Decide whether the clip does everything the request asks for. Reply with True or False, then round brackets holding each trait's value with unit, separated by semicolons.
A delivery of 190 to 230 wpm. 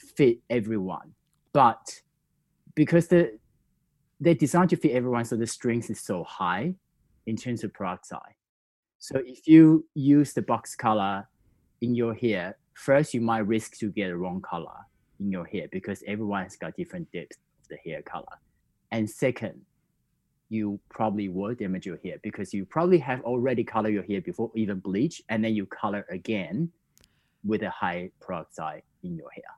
False (170 wpm)